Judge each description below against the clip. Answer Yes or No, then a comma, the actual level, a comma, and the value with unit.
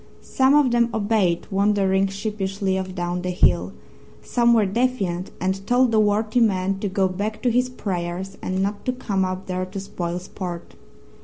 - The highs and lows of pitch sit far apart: No, average, 2.9 semitones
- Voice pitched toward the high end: Yes, high, 195 Hz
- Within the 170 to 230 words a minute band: Yes, average, 175 wpm